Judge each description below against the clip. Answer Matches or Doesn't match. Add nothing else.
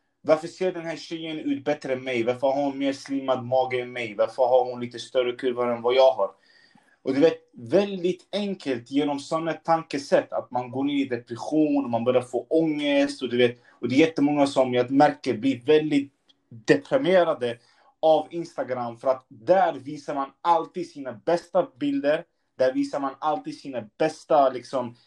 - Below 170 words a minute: Doesn't match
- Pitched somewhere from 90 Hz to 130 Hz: Doesn't match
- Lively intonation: Doesn't match